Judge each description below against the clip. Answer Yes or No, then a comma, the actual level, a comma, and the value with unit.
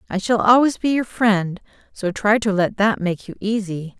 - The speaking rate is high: Yes, fast, 210 wpm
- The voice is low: No, high, 205 Hz